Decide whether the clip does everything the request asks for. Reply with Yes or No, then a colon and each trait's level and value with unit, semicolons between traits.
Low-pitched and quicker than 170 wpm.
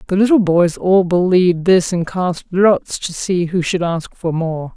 No: medium, 180 Hz; average, 200 wpm